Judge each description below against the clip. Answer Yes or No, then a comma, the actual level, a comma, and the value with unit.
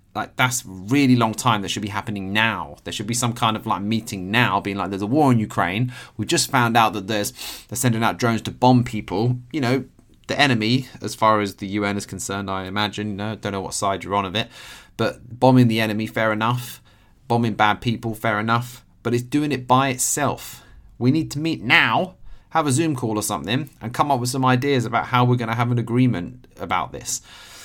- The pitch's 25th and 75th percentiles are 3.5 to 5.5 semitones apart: No, average, 3.1 semitones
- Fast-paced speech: Yes, fast, 230 wpm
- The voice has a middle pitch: No, low, 115 Hz